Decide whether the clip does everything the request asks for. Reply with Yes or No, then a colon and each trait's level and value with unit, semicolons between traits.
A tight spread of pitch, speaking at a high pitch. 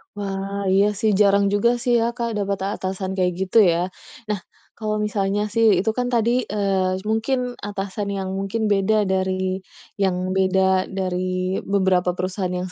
Yes: narrow, 2.1 semitones; high, 195 Hz